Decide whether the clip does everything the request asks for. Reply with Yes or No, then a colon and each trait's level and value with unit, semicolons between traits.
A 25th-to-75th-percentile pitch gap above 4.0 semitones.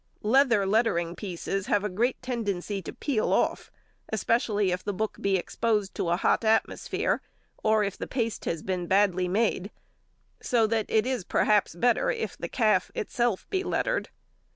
No: average, 3.3 semitones